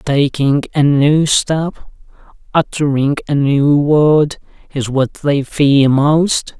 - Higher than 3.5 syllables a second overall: No, 3.0 syllables/s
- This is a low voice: No, medium, 145 Hz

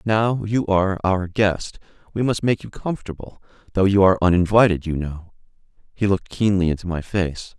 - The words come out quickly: No, average, 165 wpm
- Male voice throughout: Yes, male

